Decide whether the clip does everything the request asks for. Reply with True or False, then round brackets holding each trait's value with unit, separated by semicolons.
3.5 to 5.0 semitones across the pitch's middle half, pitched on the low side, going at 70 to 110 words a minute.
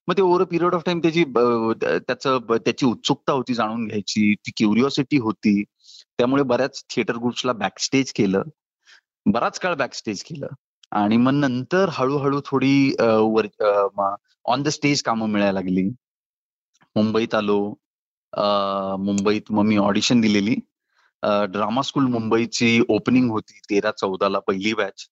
False (4.7 semitones; 115 Hz; 130 wpm)